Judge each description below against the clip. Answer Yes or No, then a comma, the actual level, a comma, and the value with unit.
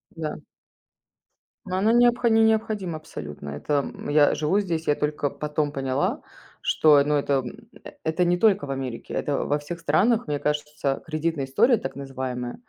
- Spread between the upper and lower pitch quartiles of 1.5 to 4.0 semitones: No, average, 4.6 semitones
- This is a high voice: No, medium, 150 Hz